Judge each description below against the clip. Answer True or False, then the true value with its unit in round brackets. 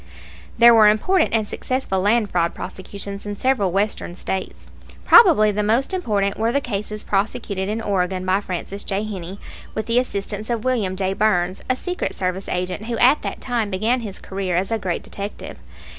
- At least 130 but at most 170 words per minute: False (180 wpm)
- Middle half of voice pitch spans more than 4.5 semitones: False (3.3 semitones)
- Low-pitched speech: False (205 Hz)